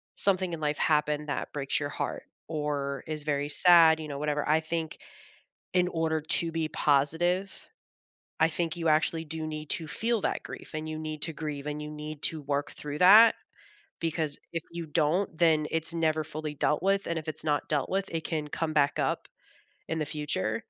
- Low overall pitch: No, medium, 155 Hz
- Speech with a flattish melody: Yes, narrow, 1.8 semitones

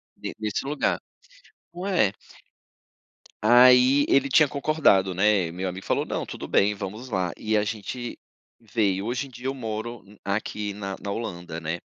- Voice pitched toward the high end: No, low, 110 Hz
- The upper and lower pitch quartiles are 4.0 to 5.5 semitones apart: Yes, average, 4.5 semitones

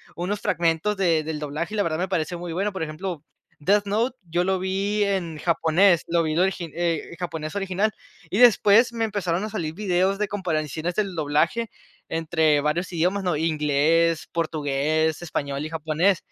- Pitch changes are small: No, average, 3.7 semitones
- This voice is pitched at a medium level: Yes, medium, 170 Hz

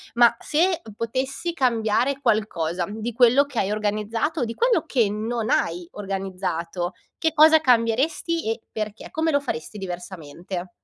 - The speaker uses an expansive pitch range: Yes, wide, 6.1 semitones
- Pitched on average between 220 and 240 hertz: Yes, high, 225 Hz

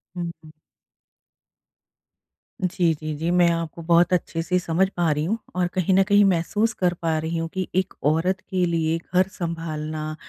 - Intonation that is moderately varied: No, narrow, 2.2 semitones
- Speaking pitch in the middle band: Yes, medium, 170 Hz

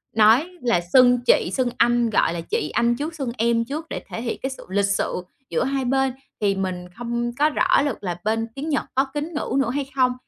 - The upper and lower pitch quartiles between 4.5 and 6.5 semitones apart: No, average, 3.7 semitones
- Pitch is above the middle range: Yes, high, 245 Hz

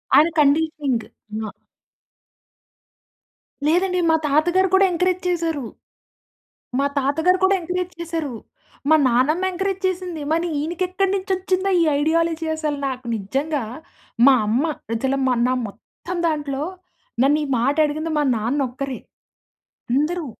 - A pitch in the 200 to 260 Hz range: No, very high, 315 Hz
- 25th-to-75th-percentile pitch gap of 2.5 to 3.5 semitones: No, average, 4.5 semitones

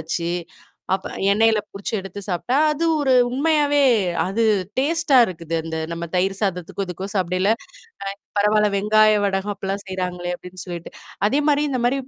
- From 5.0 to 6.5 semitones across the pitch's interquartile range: Yes, wide, 5.4 semitones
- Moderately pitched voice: No, high, 200 Hz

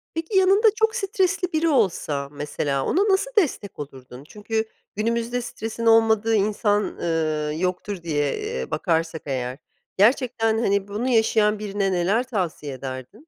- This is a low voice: No, high, 210 Hz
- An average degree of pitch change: No, wide, 7.0 semitones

